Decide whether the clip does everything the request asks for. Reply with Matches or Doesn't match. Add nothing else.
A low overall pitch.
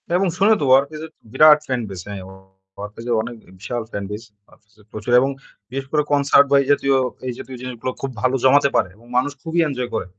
Matches